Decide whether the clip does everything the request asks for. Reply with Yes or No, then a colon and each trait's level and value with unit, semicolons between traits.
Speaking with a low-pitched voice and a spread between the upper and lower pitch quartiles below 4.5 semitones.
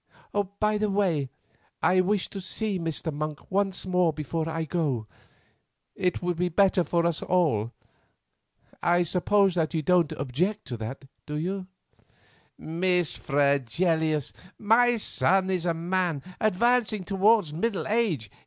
No: medium, 175 Hz; average, 3.8 semitones